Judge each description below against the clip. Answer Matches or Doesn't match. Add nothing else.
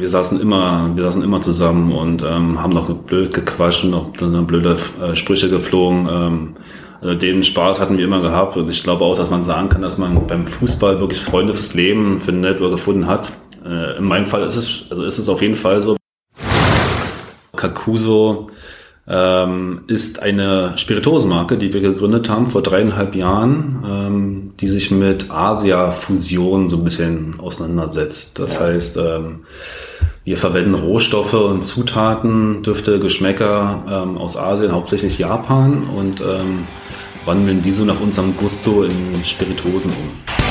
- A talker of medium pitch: Doesn't match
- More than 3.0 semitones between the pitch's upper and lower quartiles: Doesn't match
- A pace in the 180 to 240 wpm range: Doesn't match